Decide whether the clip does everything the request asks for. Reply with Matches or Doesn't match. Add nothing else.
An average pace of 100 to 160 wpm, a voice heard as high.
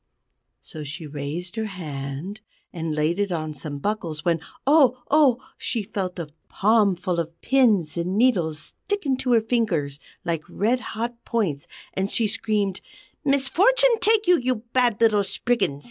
Matches